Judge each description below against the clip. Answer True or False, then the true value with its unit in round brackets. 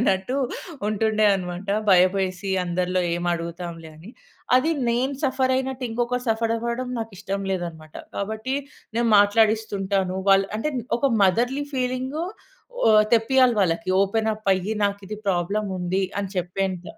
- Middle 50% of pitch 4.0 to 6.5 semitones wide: True (4.3 semitones)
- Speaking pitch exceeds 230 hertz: False (200 Hz)